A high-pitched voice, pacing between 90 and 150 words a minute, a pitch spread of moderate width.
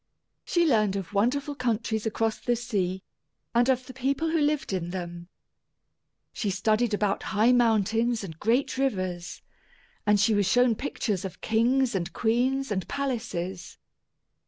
Yes: high, 225 Hz; average, 145 wpm; average, 4.4 semitones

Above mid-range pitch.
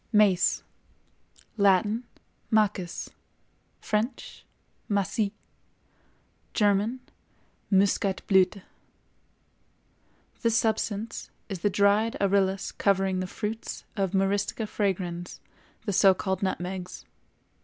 Yes: high, 200 Hz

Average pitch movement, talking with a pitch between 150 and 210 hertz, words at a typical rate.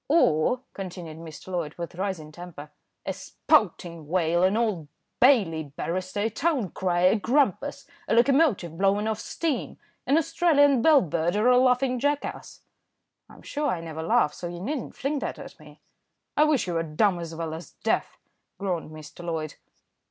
No: wide, 7.5 semitones; medium, 185 Hz; average, 165 wpm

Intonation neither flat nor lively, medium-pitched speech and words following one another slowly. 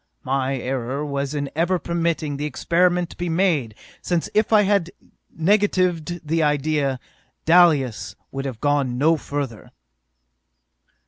Yes: average, 4.2 semitones; medium, 150 Hz; slow, 130 wpm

